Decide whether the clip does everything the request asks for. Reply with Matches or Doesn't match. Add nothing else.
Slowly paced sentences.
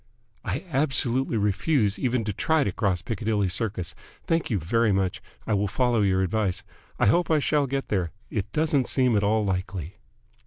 Doesn't match